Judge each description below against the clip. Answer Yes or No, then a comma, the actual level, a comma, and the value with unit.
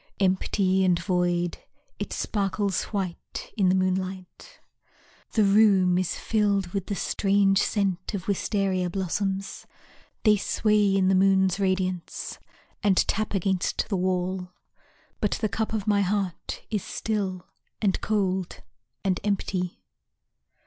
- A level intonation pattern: Yes, narrow, 1.7 semitones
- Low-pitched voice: No, high, 195 Hz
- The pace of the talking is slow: Yes, slow, 125 wpm